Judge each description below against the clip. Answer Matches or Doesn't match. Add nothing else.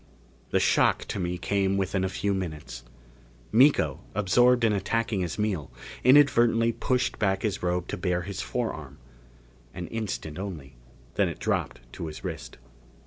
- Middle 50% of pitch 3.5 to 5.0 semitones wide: Matches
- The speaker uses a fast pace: Doesn't match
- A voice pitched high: Doesn't match